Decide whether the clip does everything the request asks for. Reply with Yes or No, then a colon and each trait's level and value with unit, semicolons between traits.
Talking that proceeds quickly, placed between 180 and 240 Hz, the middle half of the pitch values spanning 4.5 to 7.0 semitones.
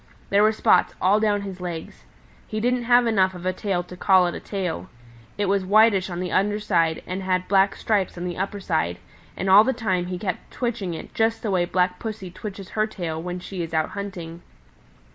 No: fast, 220 wpm; high, 190 Hz; average, 2.7 semitones